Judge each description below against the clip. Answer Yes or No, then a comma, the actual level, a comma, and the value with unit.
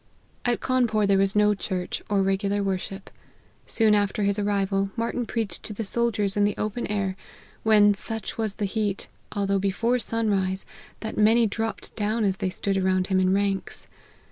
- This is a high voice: Yes, high, 205 Hz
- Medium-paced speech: Yes, average, 175 wpm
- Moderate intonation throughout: No, narrow, 2.1 semitones